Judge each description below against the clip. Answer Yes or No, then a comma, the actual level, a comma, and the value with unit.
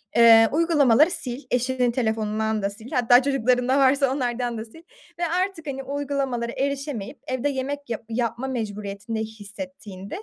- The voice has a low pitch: No, very high, 250 Hz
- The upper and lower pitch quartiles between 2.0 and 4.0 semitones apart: Yes, average, 3.7 semitones